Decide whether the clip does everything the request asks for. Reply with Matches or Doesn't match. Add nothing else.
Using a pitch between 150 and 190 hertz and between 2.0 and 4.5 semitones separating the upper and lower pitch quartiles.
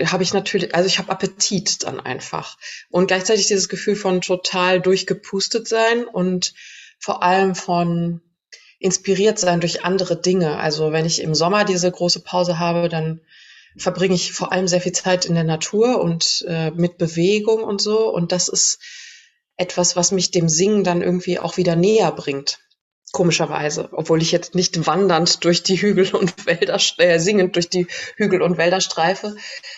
Matches